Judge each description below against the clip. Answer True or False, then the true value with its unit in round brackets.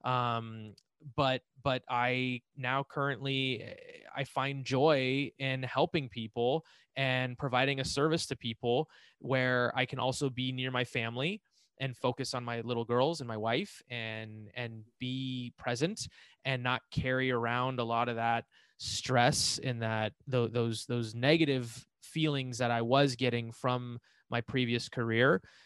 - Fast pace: False (145 wpm)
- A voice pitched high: False (125 Hz)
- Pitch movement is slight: True (2.2 semitones)